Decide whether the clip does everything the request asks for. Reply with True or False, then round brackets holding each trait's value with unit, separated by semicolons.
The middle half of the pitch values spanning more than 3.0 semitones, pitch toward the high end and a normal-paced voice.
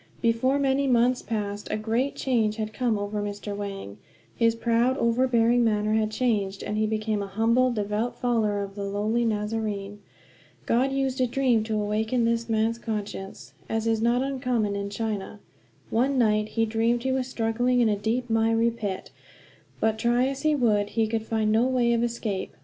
False (2.4 semitones; 225 Hz; 180 wpm)